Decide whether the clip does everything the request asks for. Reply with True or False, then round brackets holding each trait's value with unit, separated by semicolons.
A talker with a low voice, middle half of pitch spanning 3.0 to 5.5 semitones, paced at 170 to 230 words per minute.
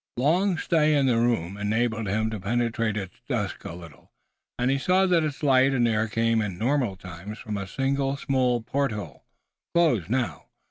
True (120 Hz; 4.6 semitones; 180 wpm)